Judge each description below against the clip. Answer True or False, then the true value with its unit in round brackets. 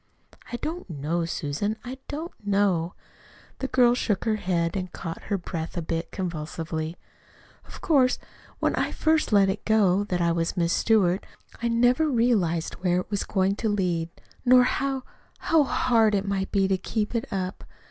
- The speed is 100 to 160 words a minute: False (175 wpm)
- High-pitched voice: True (200 Hz)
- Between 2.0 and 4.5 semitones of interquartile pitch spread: False (5.6 semitones)